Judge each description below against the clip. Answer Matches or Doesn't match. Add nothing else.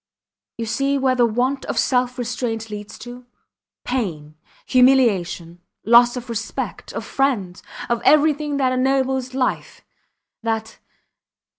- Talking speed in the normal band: Doesn't match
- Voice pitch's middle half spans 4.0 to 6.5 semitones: Doesn't match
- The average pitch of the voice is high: Matches